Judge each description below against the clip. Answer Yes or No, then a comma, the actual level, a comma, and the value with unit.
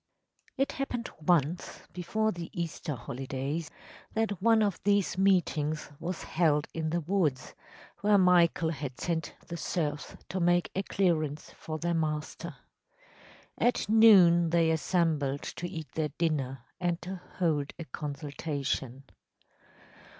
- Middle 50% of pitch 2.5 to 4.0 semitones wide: Yes, average, 3.3 semitones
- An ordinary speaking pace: No, slow, 130 wpm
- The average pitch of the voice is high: No, medium, 165 Hz